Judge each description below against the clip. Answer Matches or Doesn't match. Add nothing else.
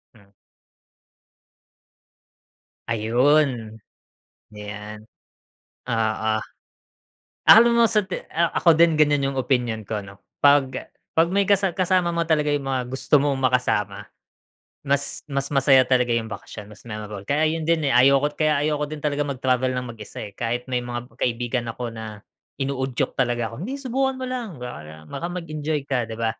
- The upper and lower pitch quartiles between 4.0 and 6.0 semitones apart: Matches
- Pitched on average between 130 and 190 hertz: Matches